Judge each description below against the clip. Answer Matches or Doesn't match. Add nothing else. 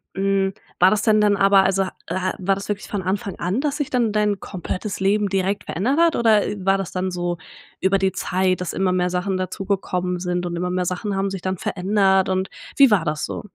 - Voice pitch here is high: Matches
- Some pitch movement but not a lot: Doesn't match